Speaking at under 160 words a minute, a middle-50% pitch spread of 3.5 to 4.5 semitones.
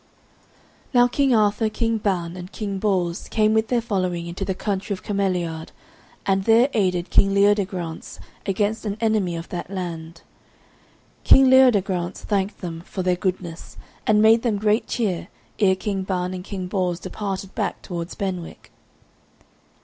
No: average, 150 wpm; average, 3.0 semitones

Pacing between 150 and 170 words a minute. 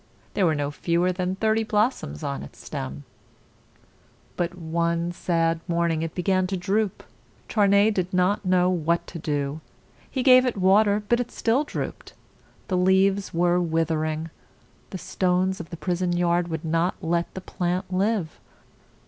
Yes: average, 160 wpm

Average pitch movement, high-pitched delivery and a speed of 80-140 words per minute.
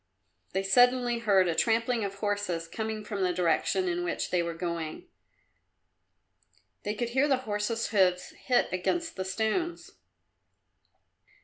Yes: average, 4.4 semitones; high, 205 Hz; slow, 135 wpm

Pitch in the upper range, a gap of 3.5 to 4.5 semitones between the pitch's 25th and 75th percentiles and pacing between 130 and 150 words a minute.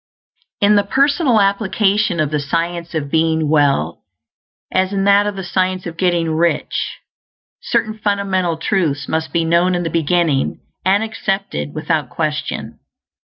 No: medium, 175 Hz; average, 3.8 semitones; average, 145 wpm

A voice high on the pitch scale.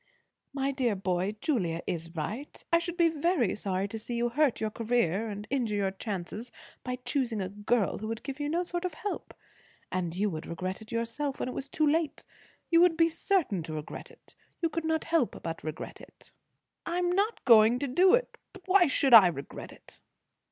Yes: high, 240 Hz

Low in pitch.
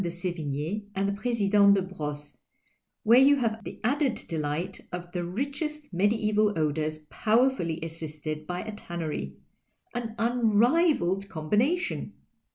No: high, 200 Hz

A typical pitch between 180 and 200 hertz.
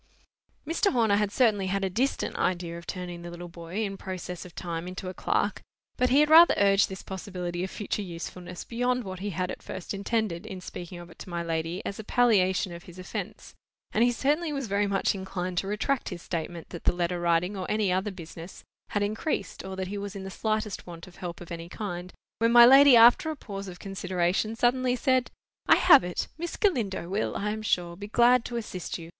Yes: high, 190 Hz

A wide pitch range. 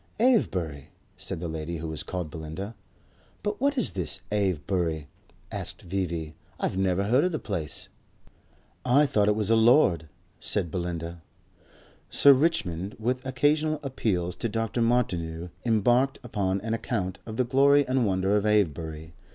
Yes: wide, 6.6 semitones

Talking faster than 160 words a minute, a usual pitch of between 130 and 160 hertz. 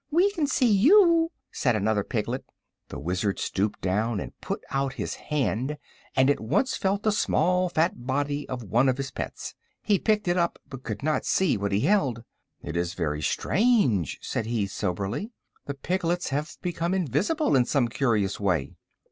Yes: average, 180 wpm; low, 135 Hz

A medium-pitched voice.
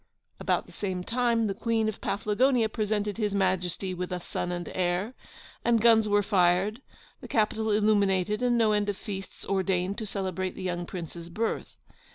No: high, 205 Hz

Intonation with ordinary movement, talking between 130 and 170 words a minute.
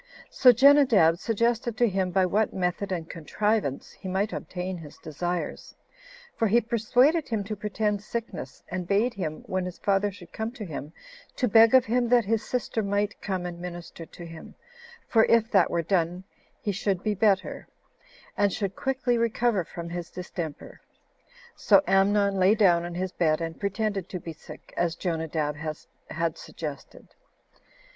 Yes: average, 4.2 semitones; average, 165 wpm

